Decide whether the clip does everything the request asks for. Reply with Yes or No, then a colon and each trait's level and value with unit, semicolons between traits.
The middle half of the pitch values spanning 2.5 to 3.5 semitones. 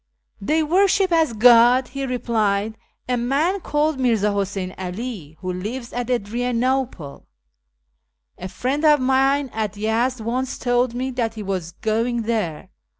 No: average, 3.9 semitones